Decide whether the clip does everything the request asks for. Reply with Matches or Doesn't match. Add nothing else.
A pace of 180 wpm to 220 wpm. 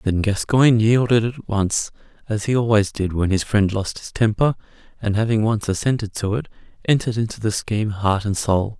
Matches